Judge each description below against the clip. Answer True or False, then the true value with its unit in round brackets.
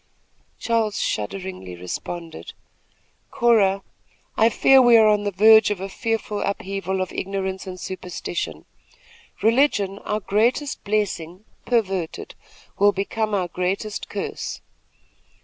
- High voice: True (200 Hz)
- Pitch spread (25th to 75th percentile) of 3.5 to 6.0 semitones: False (2.7 semitones)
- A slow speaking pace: True (115 wpm)